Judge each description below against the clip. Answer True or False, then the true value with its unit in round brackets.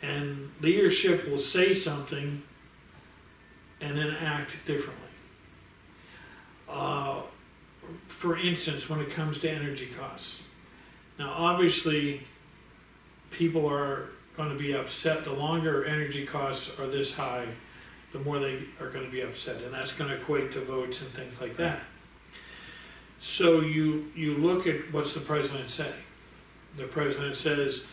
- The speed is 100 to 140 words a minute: True (135 wpm)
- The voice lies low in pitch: False (145 Hz)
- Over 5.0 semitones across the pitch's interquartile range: False (2.4 semitones)